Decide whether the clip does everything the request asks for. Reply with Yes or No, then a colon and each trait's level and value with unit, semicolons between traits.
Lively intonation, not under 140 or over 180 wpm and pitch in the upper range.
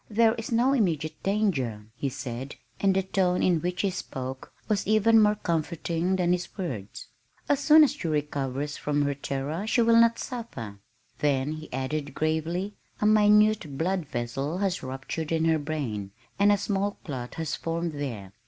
No: wide, 6.4 semitones; average, 170 wpm; medium, 165 Hz